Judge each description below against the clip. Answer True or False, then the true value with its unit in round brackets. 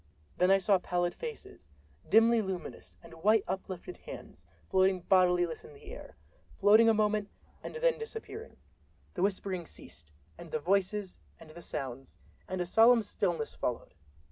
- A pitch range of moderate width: True (3.8 semitones)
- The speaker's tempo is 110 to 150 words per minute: True (145 wpm)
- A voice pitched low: False (190 Hz)